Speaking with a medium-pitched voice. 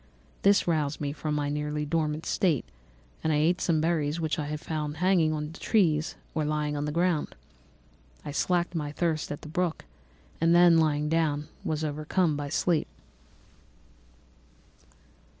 Yes: medium, 155 Hz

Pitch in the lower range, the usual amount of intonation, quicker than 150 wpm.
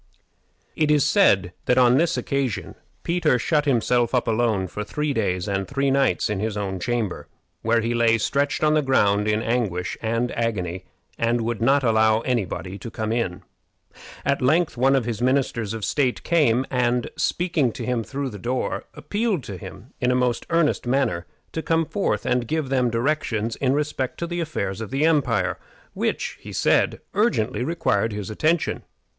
Yes: low, 125 Hz; average, 4.4 semitones; average, 180 wpm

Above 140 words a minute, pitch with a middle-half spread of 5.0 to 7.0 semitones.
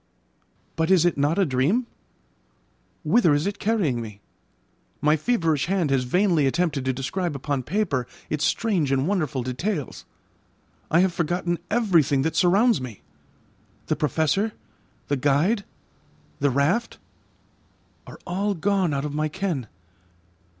No: slow, 135 wpm; wide, 5.5 semitones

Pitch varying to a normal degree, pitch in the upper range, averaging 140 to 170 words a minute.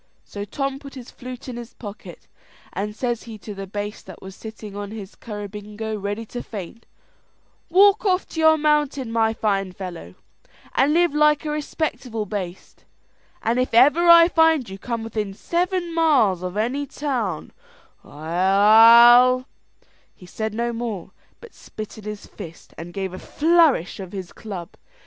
No: wide, 5.7 semitones; high, 225 Hz; average, 165 wpm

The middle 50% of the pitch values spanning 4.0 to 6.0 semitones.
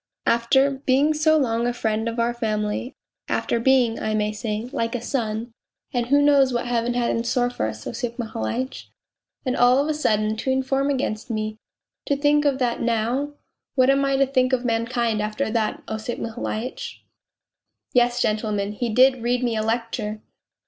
No: average, 3.1 semitones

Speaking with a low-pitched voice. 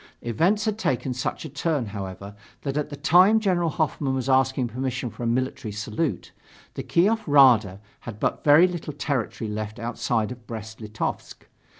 Yes: low, 130 Hz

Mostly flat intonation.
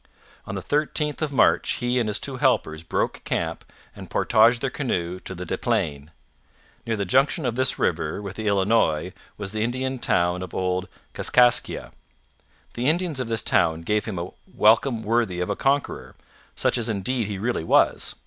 No: wide, 5.5 semitones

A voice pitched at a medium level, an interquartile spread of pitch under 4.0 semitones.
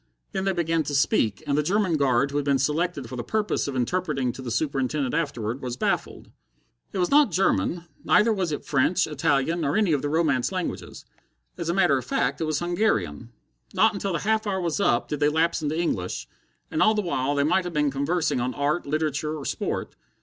No: medium, 150 Hz; average, 4.5 semitones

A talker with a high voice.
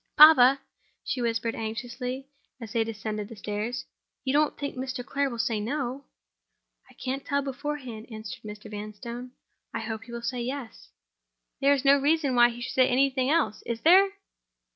Yes: very high, 250 Hz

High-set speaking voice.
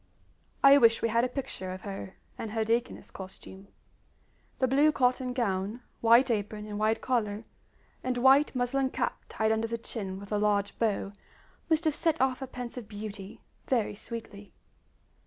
Yes: high, 230 Hz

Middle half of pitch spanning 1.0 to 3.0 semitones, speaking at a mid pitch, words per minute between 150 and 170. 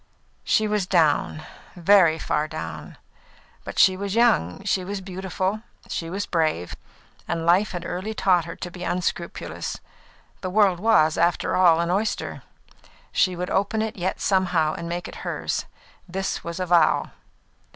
Yes: narrow, 2.5 semitones; medium, 180 Hz; average, 155 wpm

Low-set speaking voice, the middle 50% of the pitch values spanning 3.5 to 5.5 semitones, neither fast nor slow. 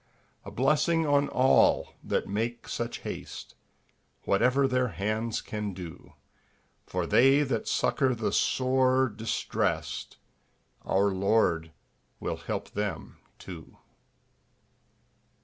No: low, 115 Hz; average, 4.5 semitones; slow, 100 wpm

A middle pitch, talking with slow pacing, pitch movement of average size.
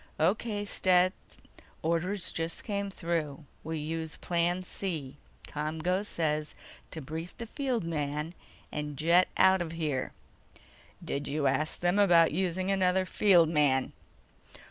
Yes: medium, 165 Hz; slow, 125 wpm; average, 3.4 semitones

